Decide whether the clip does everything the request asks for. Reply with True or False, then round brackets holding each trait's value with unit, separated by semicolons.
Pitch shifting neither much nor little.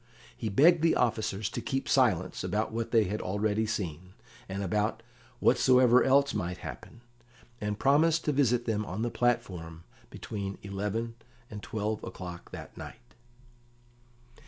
True (3.8 semitones)